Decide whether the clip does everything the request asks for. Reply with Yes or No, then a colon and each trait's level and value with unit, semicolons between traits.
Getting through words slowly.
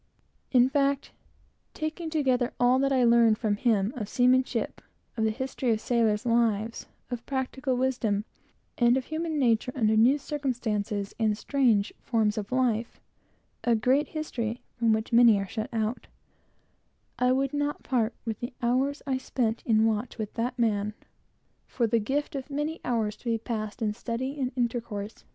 No: average, 155 wpm